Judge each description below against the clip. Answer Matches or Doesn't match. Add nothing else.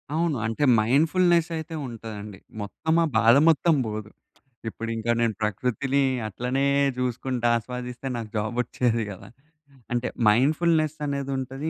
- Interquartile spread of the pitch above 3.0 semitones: Matches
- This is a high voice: Doesn't match